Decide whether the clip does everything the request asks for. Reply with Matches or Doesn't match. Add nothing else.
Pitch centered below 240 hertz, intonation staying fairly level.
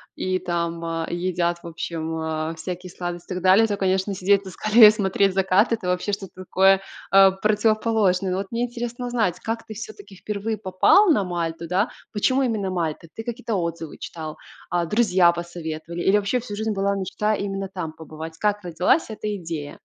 Doesn't match